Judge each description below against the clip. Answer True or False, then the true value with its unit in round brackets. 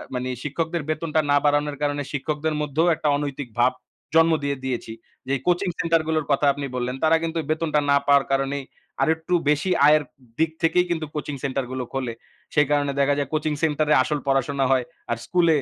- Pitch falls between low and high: True (145 Hz)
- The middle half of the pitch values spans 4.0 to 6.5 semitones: False (2.5 semitones)